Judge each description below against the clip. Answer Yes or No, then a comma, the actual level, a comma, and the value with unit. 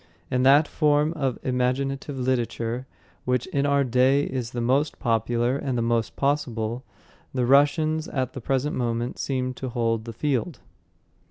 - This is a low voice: Yes, low, 130 Hz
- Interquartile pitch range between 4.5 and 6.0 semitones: No, average, 2.8 semitones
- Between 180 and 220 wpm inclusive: No, average, 165 wpm